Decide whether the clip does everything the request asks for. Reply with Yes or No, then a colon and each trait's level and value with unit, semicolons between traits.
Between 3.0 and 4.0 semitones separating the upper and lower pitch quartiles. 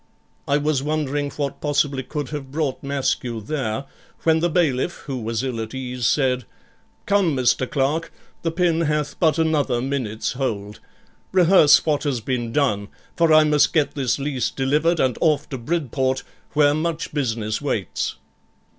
Yes: average, 3.3 semitones